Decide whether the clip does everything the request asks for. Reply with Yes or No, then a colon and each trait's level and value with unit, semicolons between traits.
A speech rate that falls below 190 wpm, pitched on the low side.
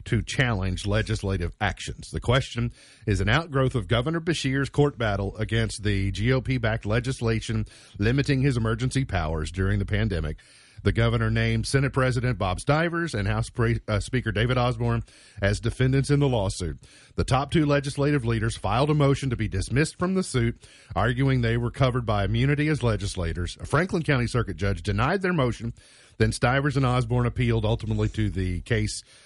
Yes: average, 170 wpm; low, 115 Hz